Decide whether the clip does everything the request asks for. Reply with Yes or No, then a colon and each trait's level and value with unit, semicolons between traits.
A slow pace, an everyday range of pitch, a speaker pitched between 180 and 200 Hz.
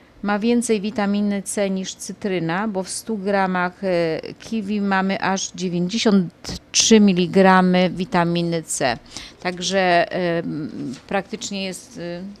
No: slow, 105 wpm; narrow, 2.2 semitones; high, 190 Hz